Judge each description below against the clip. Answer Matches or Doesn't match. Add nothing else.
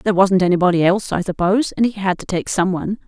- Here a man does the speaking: Doesn't match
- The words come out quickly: Matches